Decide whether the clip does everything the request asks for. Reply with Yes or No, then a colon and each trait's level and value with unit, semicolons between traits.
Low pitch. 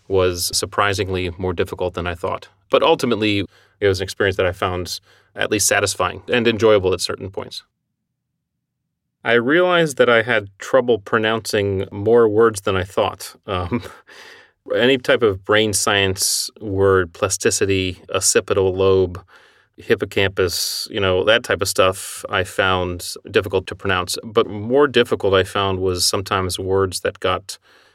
Yes: low, 100 Hz